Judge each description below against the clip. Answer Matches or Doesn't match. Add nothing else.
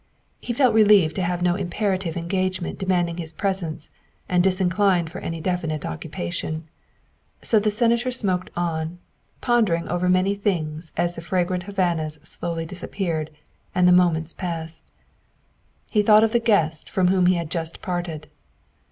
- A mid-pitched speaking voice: Matches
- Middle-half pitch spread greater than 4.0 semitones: Doesn't match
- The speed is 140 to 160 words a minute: Matches